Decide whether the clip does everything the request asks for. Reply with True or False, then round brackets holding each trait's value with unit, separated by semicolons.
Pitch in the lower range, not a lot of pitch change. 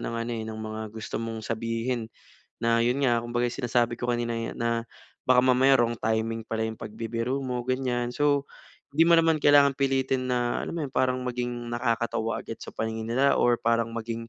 True (120 Hz; 2.0 semitones)